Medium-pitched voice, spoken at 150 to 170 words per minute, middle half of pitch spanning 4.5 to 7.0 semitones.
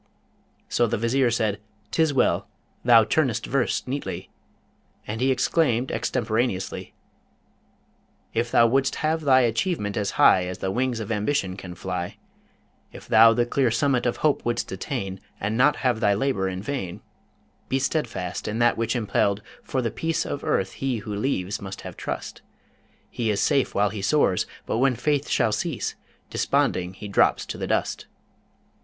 No: low, 115 Hz; average, 165 wpm; average, 4.8 semitones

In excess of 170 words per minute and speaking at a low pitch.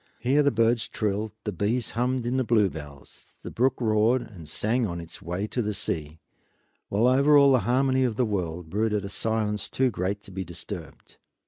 Yes: average, 195 wpm; low, 110 Hz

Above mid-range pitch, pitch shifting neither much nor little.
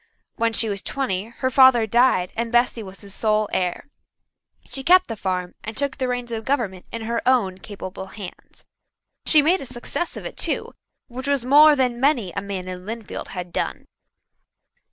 Yes: high, 230 Hz; average, 4.9 semitones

